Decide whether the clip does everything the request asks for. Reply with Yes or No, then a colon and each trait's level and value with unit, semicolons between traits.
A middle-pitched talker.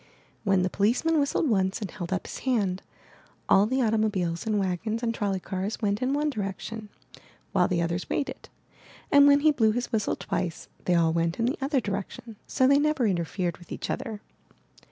No: high, 210 Hz